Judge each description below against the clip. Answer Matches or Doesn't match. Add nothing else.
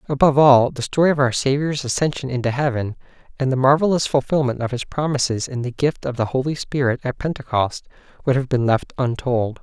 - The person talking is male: Matches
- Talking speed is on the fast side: Doesn't match